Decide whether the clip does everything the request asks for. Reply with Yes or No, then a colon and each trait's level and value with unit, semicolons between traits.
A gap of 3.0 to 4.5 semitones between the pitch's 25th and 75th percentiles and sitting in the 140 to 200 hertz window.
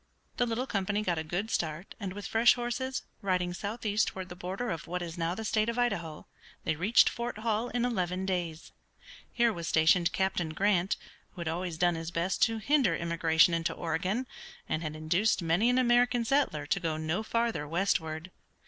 No: average, 5.2 semitones; medium, 185 Hz